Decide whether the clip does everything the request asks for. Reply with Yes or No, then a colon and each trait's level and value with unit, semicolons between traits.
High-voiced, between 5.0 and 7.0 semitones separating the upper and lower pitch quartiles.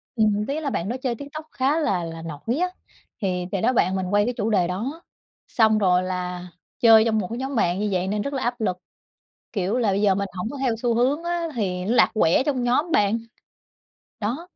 Yes: high, 220 Hz; wide, 5.5 semitones